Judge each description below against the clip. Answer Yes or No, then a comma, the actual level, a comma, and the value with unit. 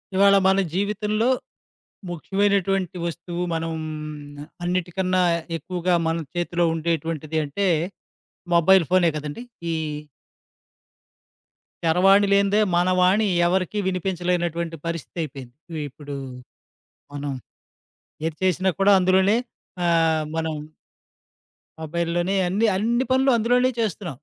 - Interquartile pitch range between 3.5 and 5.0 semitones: No, average, 3.0 semitones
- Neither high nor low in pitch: Yes, medium, 180 Hz